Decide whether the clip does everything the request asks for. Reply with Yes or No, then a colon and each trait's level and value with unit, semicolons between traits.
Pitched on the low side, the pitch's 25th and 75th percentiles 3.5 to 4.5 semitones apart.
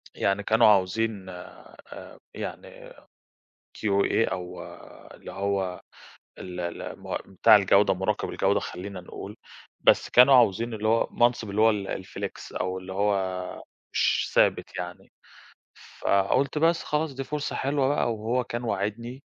Yes: low, 105 Hz; average, 3.8 semitones